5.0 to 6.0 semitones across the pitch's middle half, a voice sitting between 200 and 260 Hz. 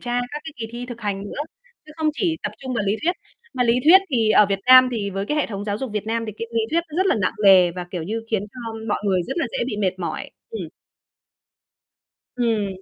No: average, 4.3 semitones; high, 225 Hz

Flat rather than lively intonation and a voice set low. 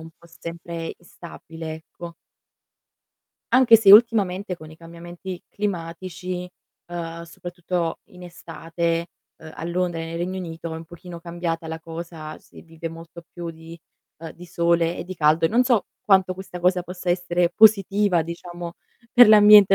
No: narrow, 1.7 semitones; medium, 175 Hz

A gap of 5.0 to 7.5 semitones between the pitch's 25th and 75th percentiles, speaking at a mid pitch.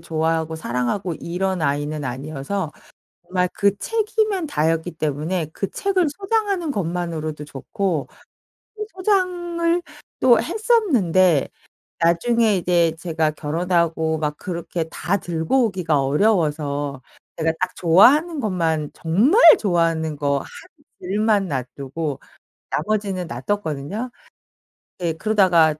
Yes: wide, 5.4 semitones; medium, 175 Hz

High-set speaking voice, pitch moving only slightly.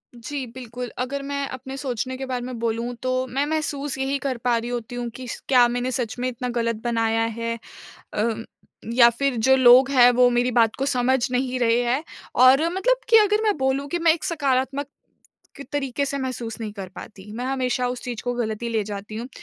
Yes: very high, 250 Hz; narrow, 2.3 semitones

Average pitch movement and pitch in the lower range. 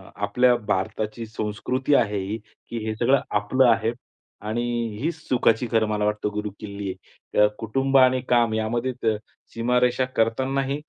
Yes: average, 3.2 semitones; low, 115 Hz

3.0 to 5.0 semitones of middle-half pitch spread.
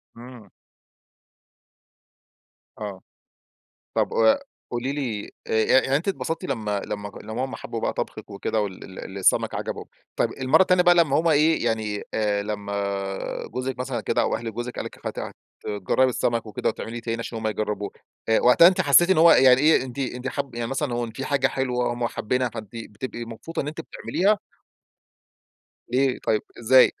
Yes: average, 4.0 semitones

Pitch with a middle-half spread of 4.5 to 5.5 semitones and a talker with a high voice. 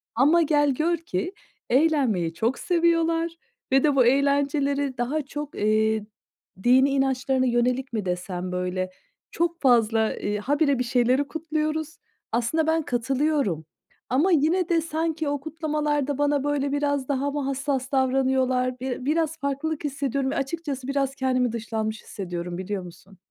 No: average, 3.8 semitones; very high, 275 Hz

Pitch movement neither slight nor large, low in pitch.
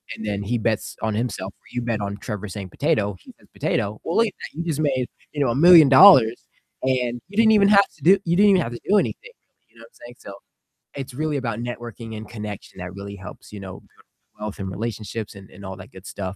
No: wide, 6.0 semitones; low, 115 Hz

